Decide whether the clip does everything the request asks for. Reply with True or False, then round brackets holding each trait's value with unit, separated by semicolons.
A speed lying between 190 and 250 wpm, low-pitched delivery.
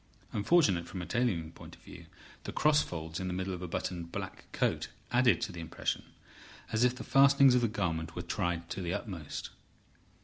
True (200 wpm; 95 Hz)